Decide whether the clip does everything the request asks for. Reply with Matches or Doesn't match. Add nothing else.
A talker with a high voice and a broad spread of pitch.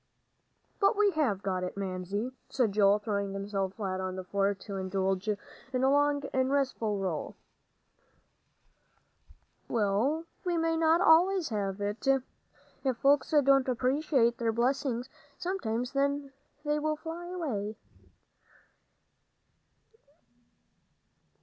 Matches